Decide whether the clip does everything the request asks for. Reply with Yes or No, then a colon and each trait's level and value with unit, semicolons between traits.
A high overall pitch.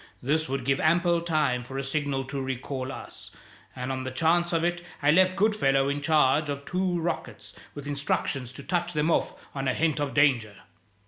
No: medium, 145 Hz